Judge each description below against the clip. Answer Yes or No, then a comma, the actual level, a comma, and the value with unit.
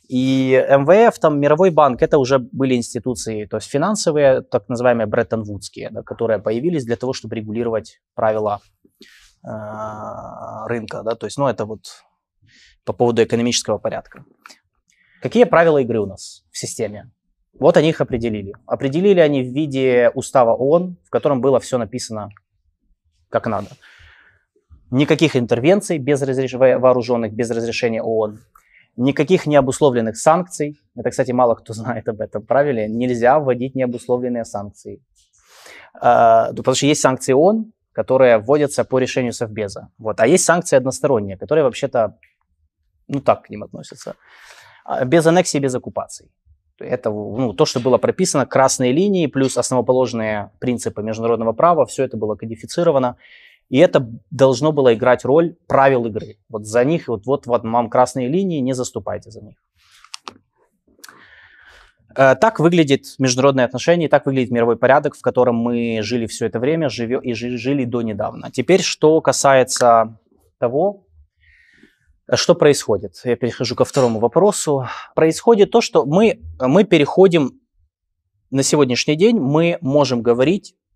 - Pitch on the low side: Yes, low, 125 Hz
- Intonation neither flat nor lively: Yes, average, 4.3 semitones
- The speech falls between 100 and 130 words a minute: No, average, 140 wpm